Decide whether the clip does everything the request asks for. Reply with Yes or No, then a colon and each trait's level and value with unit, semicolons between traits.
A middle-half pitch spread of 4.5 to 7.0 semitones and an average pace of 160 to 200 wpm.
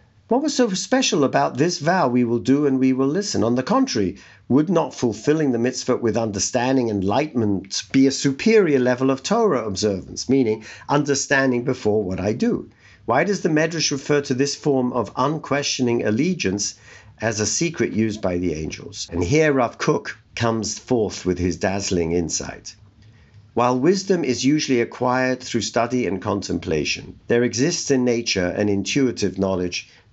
Yes: average, 5.1 semitones; average, 165 wpm